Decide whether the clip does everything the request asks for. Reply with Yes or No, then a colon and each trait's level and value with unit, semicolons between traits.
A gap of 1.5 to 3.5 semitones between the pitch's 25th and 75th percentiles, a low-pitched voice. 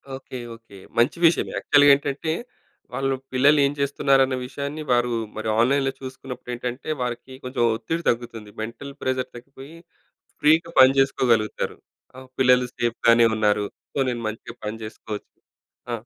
Yes: average, 2.8 semitones; low, 130 Hz